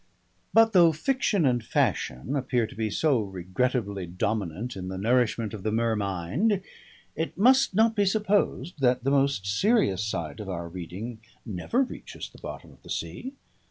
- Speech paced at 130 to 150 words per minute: No, average, 165 wpm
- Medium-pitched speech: No, low, 120 Hz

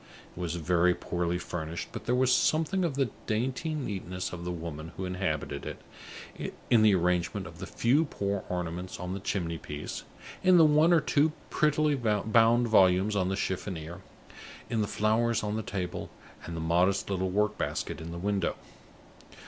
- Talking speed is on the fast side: No, average, 175 wpm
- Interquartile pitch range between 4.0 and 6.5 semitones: Yes, average, 5.1 semitones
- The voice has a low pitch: Yes, low, 100 Hz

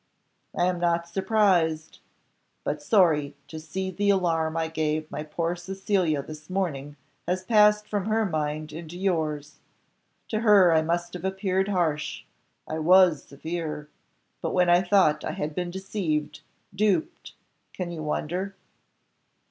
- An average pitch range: Yes, average, 3.5 semitones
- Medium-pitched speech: Yes, medium, 175 Hz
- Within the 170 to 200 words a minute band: No, average, 145 wpm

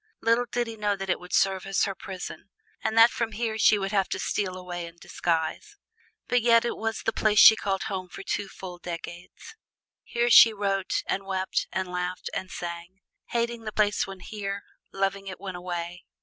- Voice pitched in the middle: No, high, 195 Hz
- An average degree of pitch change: Yes, average, 3.2 semitones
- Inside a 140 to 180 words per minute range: No, average, 200 wpm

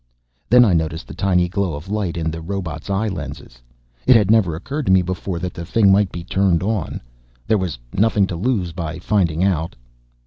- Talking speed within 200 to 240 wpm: Yes, fast, 205 wpm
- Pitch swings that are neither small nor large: Yes, average, 3.3 semitones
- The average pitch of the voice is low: Yes, very low, 90 Hz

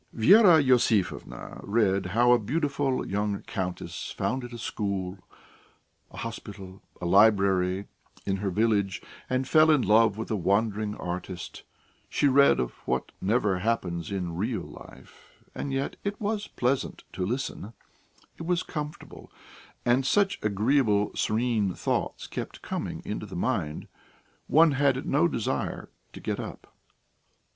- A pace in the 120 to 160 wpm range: Yes, slow, 135 wpm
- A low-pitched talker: Yes, low, 110 Hz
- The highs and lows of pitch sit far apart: Yes, wide, 5.7 semitones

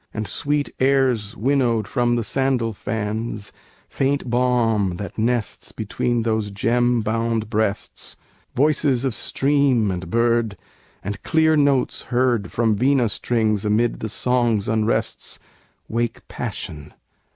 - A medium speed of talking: No, slow, 120 wpm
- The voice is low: Yes, low, 115 Hz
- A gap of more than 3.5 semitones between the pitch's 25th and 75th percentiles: No, average, 2.8 semitones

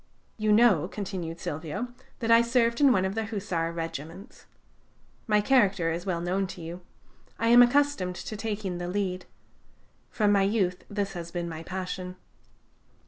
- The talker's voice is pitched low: No, high, 195 Hz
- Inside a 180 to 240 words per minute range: No, average, 160 wpm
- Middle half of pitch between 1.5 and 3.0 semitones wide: No, average, 3.9 semitones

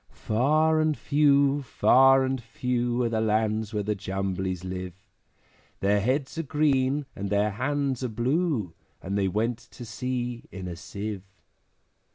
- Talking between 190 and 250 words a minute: No, average, 150 wpm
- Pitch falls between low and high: No, low, 120 Hz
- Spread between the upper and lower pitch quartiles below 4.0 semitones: No, average, 4.9 semitones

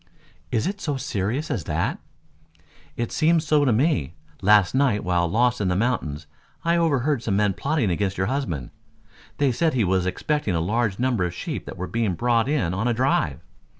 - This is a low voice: Yes, low, 115 Hz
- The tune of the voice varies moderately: No, wide, 6.8 semitones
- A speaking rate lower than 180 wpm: No, average, 190 wpm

